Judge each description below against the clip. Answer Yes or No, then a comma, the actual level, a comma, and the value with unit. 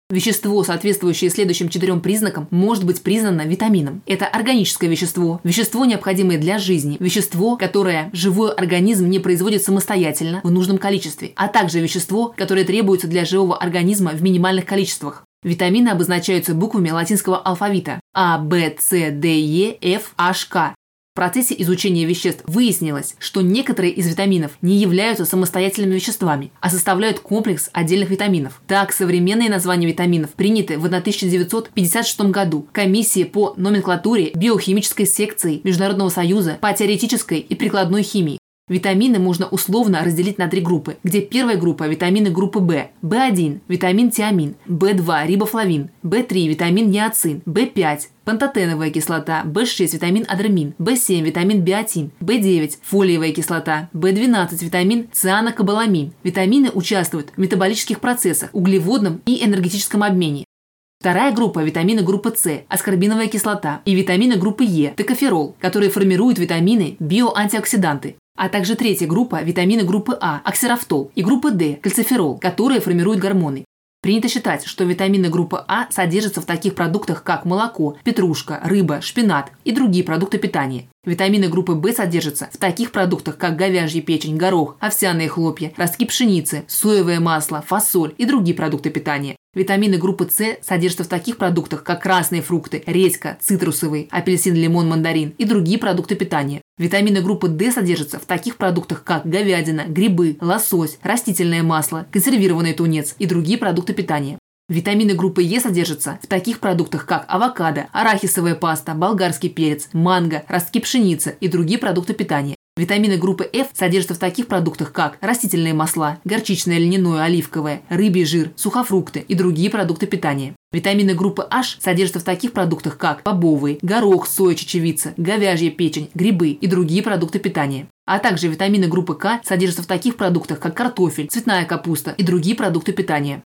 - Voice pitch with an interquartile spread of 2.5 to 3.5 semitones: Yes, average, 3.2 semitones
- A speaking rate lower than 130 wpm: No, average, 145 wpm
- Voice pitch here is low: No, medium, 185 Hz